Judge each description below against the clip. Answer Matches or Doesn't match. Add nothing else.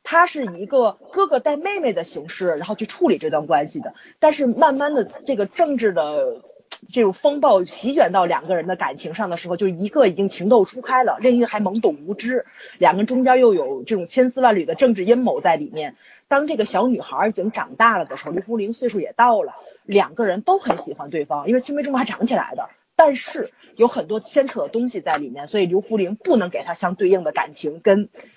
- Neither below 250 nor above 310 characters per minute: Doesn't match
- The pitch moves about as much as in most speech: Doesn't match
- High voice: Matches